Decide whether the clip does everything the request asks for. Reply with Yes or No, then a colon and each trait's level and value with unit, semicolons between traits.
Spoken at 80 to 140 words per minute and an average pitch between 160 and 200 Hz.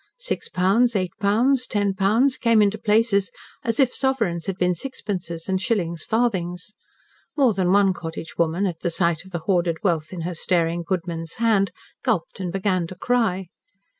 No: average, 170 wpm; high, 190 Hz